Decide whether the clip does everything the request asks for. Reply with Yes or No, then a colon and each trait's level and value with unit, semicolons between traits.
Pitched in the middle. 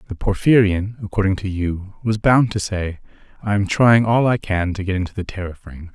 No: low, 100 Hz